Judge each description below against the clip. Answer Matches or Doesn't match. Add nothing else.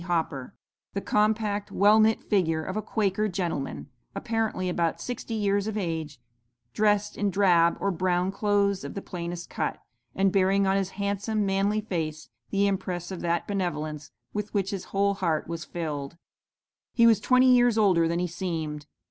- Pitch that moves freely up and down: Doesn't match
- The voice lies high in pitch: Matches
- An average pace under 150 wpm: Doesn't match